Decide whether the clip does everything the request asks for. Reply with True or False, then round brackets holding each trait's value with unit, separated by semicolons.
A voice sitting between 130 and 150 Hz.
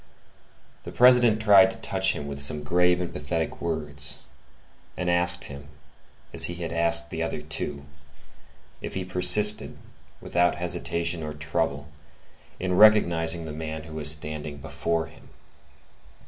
False (85 Hz)